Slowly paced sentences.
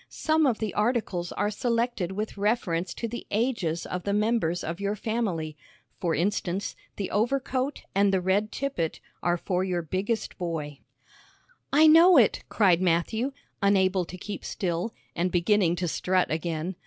No: average, 155 wpm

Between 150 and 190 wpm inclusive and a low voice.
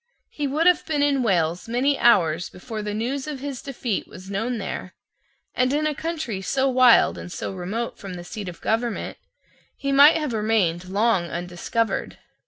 No: average, 180 wpm; high, 230 Hz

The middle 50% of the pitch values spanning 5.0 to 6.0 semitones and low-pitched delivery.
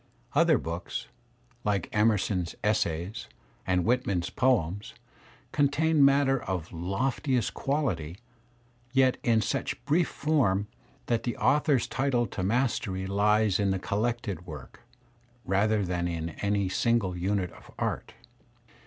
Yes: wide, 5.6 semitones; low, 105 Hz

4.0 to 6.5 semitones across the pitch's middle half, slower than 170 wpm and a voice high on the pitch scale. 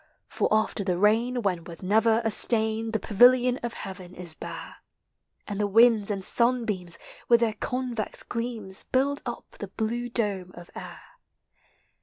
No: average, 3.4 semitones; average, 155 wpm; high, 220 Hz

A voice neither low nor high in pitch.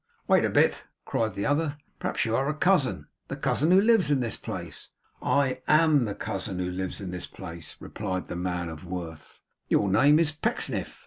No: low, 110 Hz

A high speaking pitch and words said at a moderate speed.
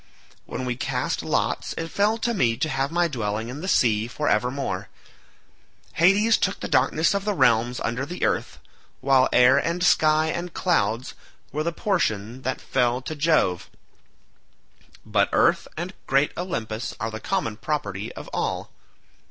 No: low, 135 Hz; average, 160 wpm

